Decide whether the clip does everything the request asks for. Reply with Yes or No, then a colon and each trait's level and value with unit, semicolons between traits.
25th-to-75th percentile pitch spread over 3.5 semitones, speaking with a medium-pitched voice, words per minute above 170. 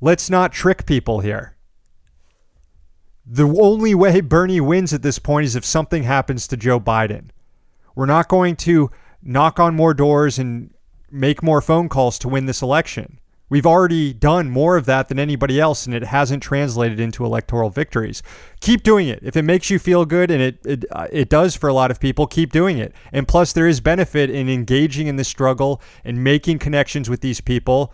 Yes: average, 4.2 semitones; medium, 145 Hz; average, 200 wpm